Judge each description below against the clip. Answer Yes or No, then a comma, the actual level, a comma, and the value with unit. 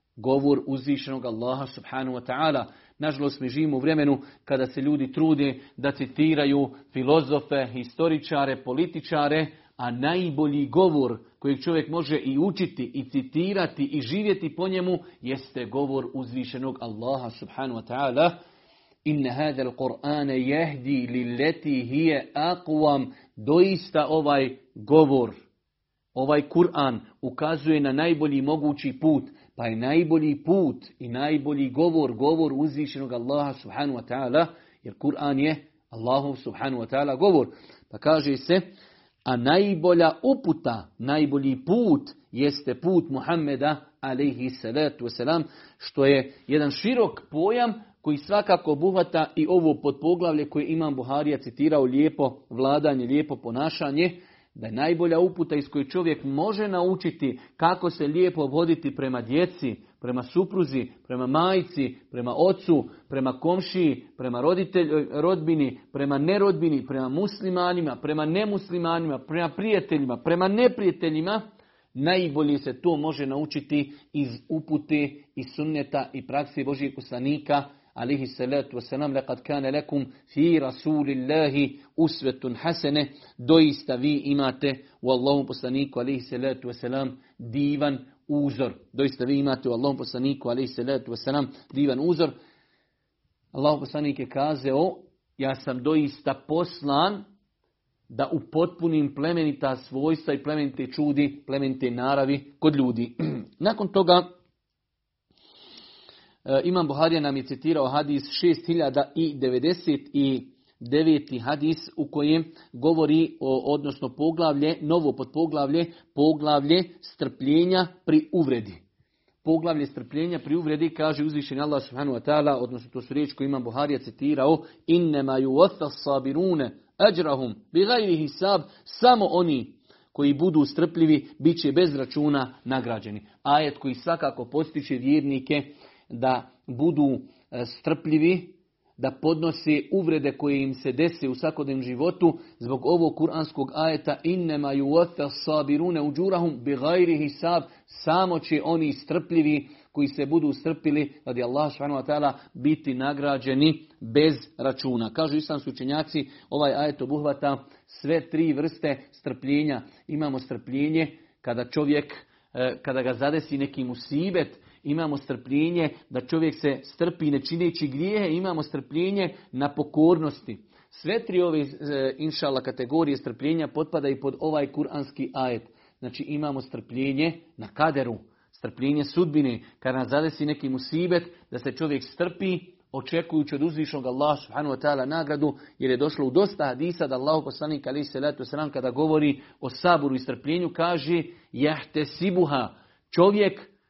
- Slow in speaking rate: No, average, 125 wpm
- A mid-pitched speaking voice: Yes, medium, 145 Hz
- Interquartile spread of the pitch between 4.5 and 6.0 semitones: No, average, 3.2 semitones